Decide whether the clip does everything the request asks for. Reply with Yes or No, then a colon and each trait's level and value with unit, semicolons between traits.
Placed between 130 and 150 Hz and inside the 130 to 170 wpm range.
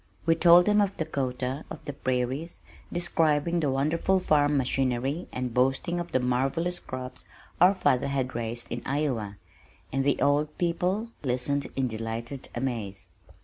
Yes: medium, 140 Hz; average, 145 wpm